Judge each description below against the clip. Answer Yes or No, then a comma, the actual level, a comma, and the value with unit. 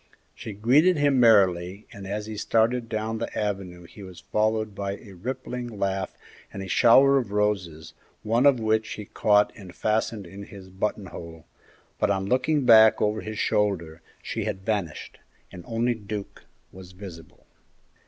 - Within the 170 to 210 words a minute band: No, average, 160 wpm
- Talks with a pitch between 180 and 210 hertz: No, low, 105 Hz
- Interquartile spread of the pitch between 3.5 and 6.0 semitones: No, average, 2.8 semitones